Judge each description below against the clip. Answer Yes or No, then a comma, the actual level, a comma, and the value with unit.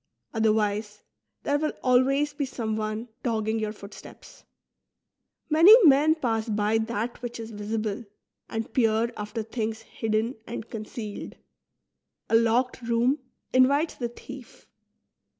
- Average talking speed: No, slow, 120 wpm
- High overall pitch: Yes, high, 225 Hz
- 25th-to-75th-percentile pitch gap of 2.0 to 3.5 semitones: Yes, average, 2.7 semitones